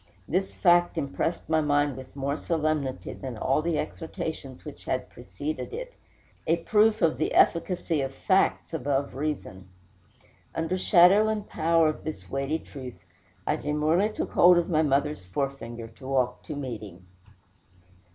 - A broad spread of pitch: No, average, 3.9 semitones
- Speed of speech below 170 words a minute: Yes, average, 150 wpm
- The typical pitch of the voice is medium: Yes, medium, 150 Hz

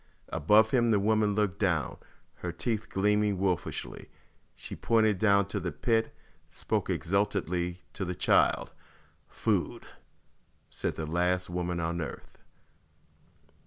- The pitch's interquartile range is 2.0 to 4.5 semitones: Yes, average, 3.2 semitones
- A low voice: Yes, very low, 95 Hz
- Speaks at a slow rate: Yes, slow, 125 wpm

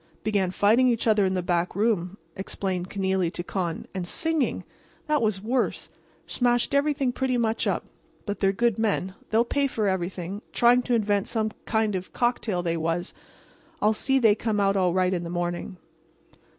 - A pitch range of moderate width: Yes, average, 4.3 semitones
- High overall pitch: Yes, high, 205 Hz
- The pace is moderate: Yes, average, 180 wpm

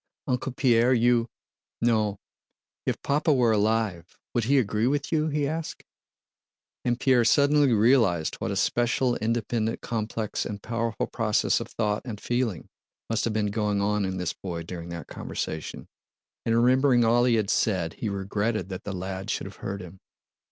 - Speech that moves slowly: No, average, 165 wpm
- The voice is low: Yes, low, 115 Hz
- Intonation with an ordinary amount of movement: Yes, average, 3.4 semitones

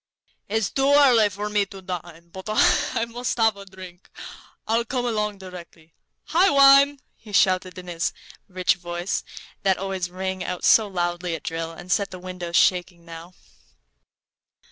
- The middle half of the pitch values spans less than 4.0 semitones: Yes, average, 3.6 semitones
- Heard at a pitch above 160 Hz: Yes, high, 190 Hz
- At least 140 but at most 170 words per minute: Yes, average, 160 wpm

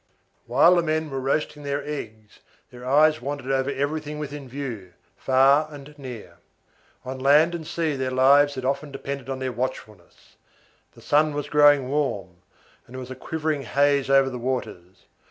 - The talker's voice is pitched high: No, medium, 140 Hz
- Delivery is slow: No, average, 170 wpm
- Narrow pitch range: Yes, narrow, 2.3 semitones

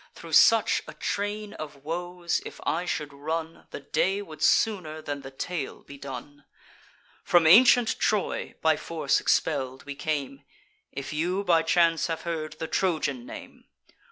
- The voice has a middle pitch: Yes, medium, 160 Hz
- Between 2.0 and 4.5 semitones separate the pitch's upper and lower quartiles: Yes, average, 3.6 semitones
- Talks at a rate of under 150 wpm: No, average, 155 wpm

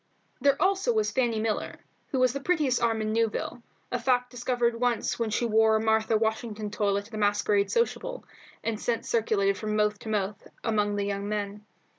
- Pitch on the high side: Yes, high, 220 Hz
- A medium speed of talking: Yes, average, 190 wpm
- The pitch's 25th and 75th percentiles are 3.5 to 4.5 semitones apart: No, average, 2.8 semitones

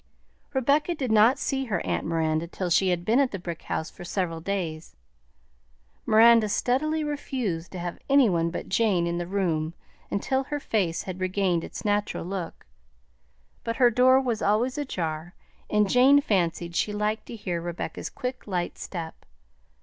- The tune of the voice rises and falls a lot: Yes, wide, 6.4 semitones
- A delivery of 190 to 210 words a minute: No, average, 165 wpm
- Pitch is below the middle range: No, high, 200 Hz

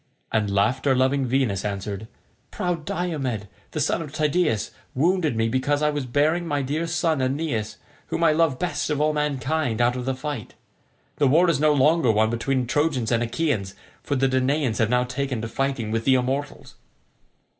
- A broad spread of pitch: No, average, 4.1 semitones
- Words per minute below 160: No, average, 180 wpm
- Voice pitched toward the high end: No, low, 135 Hz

